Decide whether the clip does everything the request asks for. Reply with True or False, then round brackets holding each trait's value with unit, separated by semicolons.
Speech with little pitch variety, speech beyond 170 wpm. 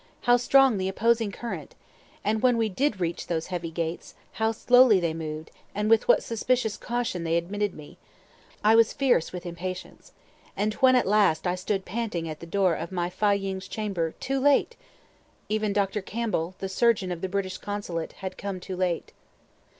False (4.2 semitones; 180 wpm)